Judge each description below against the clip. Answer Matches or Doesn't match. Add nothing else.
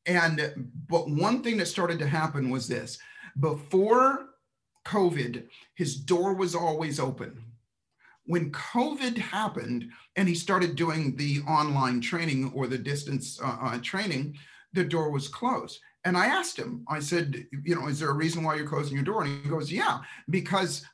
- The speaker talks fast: Doesn't match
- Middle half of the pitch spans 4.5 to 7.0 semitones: Matches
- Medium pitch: Matches